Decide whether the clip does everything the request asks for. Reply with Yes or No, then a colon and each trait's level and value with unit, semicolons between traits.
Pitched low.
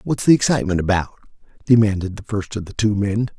Yes: low, 105 Hz